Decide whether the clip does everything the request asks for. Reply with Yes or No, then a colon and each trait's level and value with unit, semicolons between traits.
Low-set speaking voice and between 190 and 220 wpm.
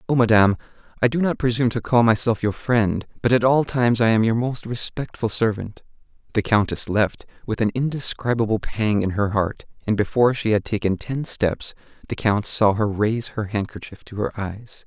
Yes: low, 110 Hz; average, 195 wpm